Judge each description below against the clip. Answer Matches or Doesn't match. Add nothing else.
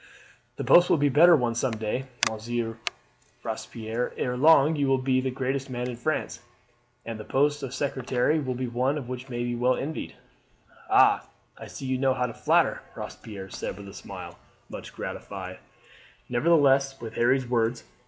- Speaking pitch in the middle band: Doesn't match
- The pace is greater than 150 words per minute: Matches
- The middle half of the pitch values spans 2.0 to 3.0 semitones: Matches